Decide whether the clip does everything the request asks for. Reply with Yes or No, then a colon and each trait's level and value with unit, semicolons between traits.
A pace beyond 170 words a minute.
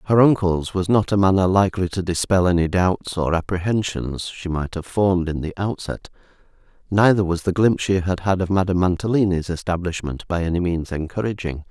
Yes: average, 180 wpm